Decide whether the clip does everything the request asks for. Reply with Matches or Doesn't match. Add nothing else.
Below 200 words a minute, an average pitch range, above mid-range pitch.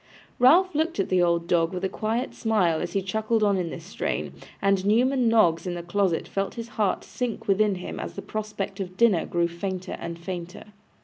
Doesn't match